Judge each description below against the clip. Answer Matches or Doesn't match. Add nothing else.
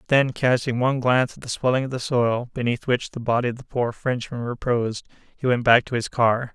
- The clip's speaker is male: Matches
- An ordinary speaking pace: Doesn't match